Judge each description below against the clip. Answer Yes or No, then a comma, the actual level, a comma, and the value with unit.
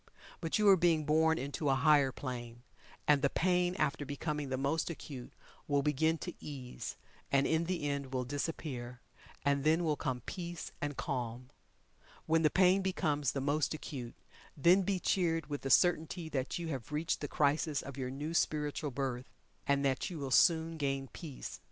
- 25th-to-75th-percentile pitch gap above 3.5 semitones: No, average, 3.2 semitones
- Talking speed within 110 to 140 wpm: No, average, 180 wpm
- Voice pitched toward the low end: No, medium, 150 Hz